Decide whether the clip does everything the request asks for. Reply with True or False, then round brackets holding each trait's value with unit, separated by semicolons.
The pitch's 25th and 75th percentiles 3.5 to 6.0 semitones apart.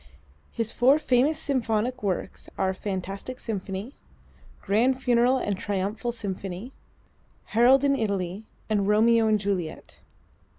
True (4.1 semitones)